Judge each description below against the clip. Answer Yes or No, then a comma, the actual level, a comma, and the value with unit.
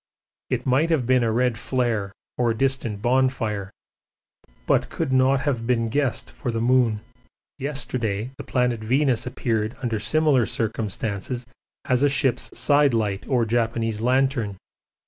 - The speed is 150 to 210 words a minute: No, average, 140 wpm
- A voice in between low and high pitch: No, low, 120 Hz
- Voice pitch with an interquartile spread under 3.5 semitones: Yes, average, 2.8 semitones